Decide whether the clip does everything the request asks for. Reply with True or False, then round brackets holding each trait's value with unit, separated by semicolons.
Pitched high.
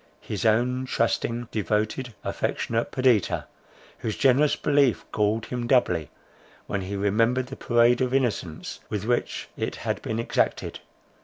False (115 Hz)